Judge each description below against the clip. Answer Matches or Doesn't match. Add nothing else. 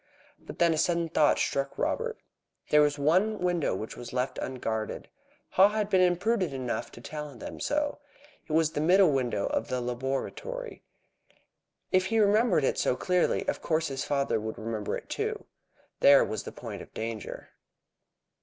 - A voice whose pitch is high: Doesn't match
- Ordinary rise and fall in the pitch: Doesn't match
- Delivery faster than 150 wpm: Matches